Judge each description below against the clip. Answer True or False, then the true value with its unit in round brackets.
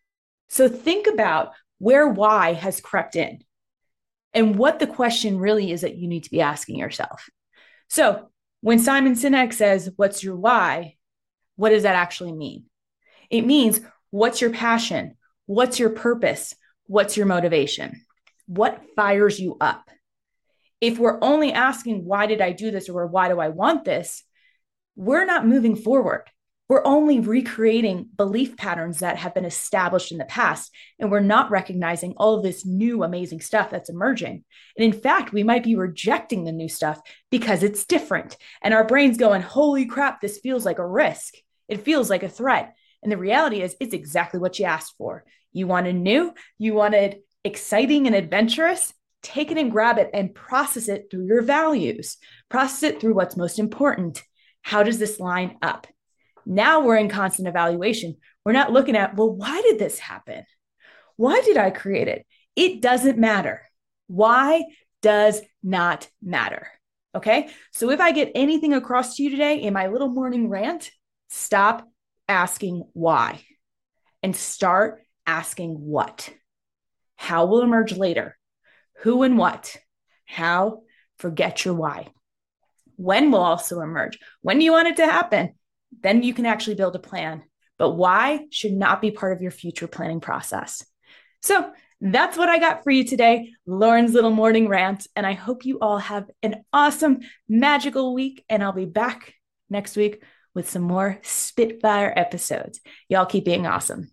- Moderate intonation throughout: False (5.7 semitones)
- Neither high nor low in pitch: False (215 Hz)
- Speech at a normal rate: True (165 wpm)